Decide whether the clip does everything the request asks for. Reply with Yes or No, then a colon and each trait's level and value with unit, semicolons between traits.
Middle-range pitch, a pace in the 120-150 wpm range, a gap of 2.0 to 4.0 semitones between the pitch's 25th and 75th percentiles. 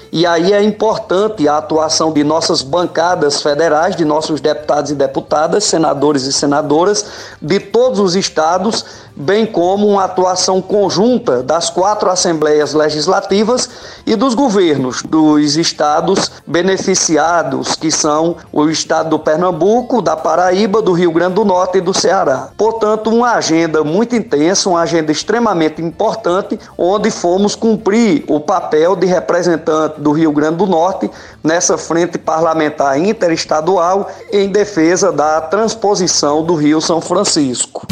No: medium, 175 Hz; average, 135 wpm; average, 4.7 semitones